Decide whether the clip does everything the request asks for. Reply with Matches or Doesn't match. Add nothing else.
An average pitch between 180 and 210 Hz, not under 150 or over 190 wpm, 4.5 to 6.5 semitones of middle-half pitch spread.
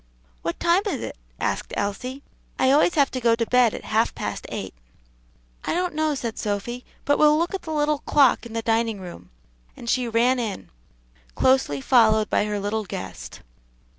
Doesn't match